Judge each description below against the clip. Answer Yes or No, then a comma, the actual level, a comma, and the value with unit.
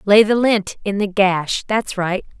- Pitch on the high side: Yes, high, 200 Hz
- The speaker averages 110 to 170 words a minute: No, average, 200 wpm